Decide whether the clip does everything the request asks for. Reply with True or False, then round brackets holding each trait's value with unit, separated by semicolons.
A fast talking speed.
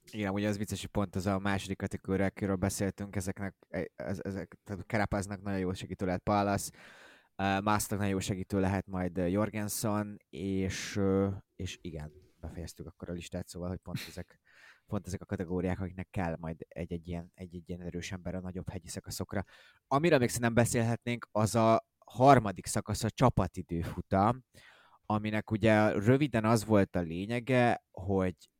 True (160 wpm)